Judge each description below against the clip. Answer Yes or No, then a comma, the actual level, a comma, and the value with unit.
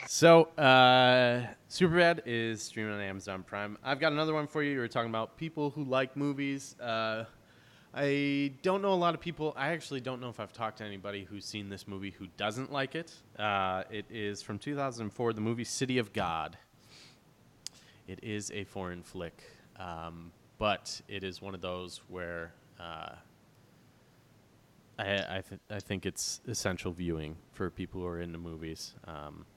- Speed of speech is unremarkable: Yes, average, 170 wpm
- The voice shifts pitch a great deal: Yes, wide, 5.8 semitones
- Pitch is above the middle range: No, low, 110 Hz